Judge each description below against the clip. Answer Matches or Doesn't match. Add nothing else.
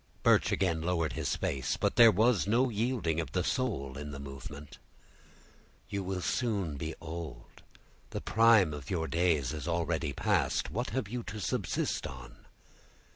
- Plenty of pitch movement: Matches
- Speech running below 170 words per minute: Matches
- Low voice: Matches